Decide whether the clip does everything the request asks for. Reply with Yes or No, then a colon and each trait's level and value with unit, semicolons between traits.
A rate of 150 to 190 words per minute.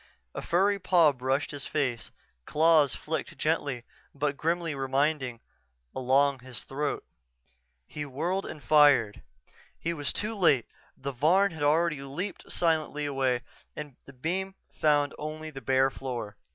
No: average, 140 wpm